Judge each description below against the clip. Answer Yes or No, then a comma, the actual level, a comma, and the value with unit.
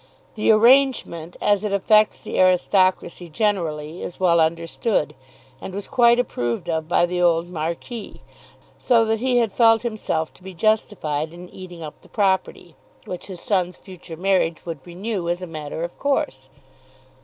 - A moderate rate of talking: Yes, average, 160 wpm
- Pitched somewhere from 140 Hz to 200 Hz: Yes, medium, 185 Hz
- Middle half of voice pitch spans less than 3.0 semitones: No, average, 4.3 semitones